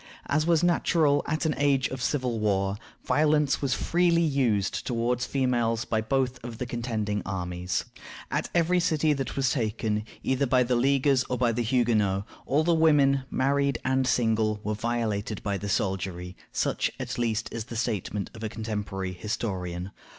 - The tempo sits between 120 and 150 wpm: No, average, 165 wpm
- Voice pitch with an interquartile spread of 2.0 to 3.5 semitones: No, average, 4.6 semitones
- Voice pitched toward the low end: Yes, low, 120 Hz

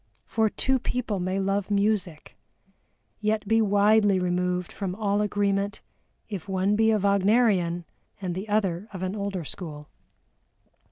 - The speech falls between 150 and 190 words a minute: No, slow, 135 wpm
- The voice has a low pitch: No, high, 200 Hz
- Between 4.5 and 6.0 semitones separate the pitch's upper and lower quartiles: No, narrow, 2.4 semitones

